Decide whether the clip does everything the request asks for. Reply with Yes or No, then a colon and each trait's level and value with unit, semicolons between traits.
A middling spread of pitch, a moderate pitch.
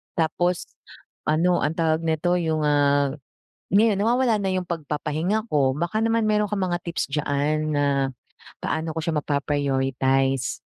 Yes: average, 3.8 semitones; medium, 160 Hz